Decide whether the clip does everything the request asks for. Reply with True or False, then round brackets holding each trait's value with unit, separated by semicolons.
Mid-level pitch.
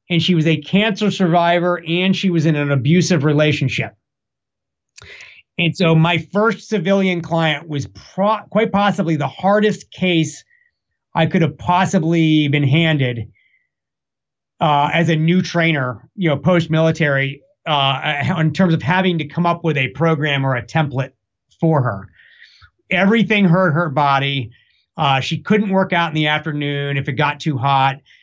True (160 Hz)